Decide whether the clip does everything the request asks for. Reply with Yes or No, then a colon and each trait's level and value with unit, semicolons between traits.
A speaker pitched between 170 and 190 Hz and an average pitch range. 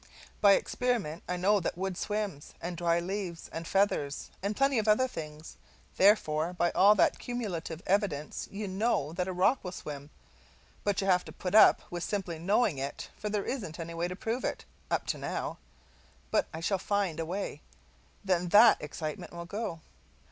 Yes: medium, 185 Hz; average, 3.8 semitones